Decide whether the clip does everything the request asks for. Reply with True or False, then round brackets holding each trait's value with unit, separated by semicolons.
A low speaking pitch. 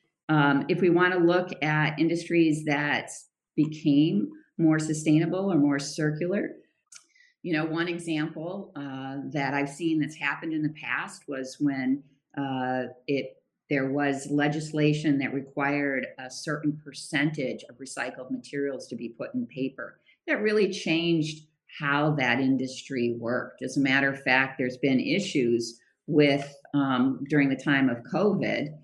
False (145 Hz)